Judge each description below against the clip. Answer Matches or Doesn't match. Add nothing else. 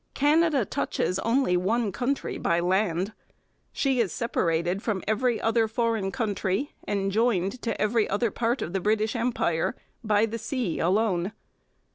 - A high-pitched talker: Matches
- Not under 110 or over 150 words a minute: Matches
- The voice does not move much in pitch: Doesn't match